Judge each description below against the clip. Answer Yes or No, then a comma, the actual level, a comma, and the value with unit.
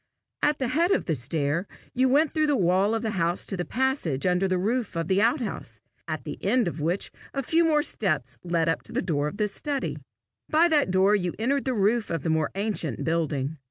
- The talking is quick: Yes, fast, 230 wpm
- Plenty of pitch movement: Yes, wide, 7.6 semitones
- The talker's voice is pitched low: No, high, 195 Hz